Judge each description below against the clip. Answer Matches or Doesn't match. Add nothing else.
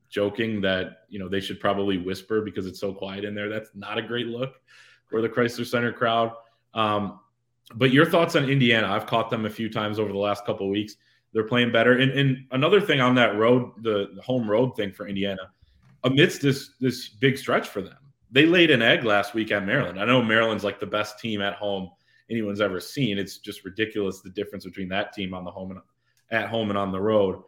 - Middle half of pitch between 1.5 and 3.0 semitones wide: Doesn't match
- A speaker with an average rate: Doesn't match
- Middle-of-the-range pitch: Doesn't match